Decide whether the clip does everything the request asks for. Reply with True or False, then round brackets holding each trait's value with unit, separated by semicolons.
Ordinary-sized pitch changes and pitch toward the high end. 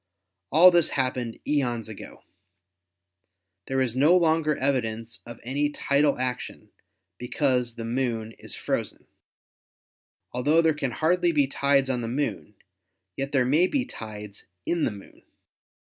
False (4.1 semitones; 135 Hz)